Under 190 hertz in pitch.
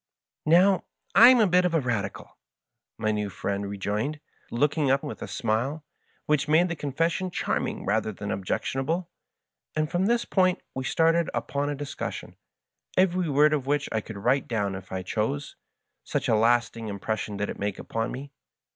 Yes: medium, 140 Hz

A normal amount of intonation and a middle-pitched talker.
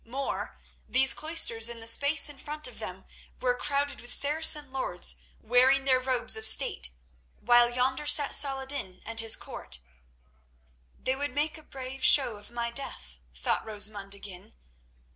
No: average, 3.9 semitones; very high, 255 Hz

